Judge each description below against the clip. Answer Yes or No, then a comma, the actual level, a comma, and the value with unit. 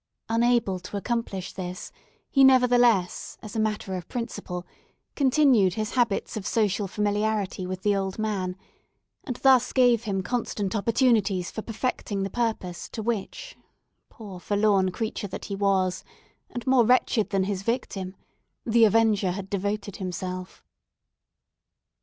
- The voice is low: No, high, 210 Hz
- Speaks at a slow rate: Yes, slow, 130 wpm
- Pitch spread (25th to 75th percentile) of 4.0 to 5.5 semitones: No, average, 3.6 semitones